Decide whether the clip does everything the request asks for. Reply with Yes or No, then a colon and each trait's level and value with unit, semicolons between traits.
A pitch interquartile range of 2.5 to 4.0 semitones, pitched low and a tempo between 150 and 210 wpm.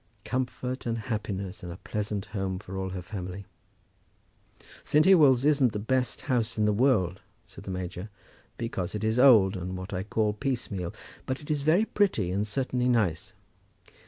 No: average, 5.0 semitones; low, 105 Hz; average, 170 wpm